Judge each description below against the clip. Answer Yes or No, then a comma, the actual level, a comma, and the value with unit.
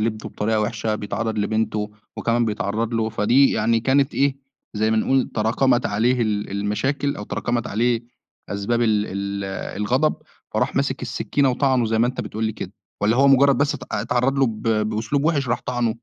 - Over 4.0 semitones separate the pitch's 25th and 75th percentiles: No, average, 3.2 semitones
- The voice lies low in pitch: Yes, low, 115 Hz